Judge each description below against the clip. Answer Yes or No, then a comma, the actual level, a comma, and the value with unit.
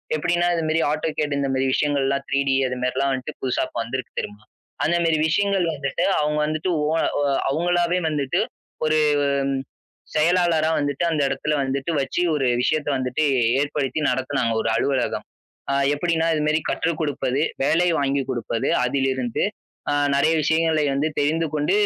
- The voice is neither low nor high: Yes, medium, 145 Hz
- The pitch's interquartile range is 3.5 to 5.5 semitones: No, average, 3.1 semitones